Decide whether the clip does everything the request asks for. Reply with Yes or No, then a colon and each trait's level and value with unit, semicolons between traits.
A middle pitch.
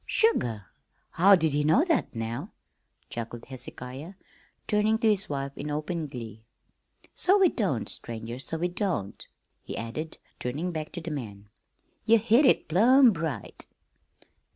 Yes: medium, 155 Hz